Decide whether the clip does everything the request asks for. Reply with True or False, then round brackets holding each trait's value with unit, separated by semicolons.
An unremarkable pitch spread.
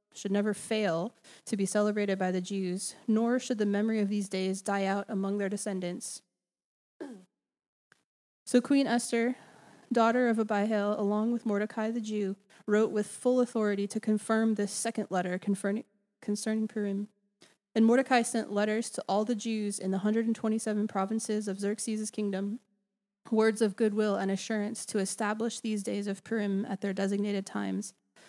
False (1.9 semitones)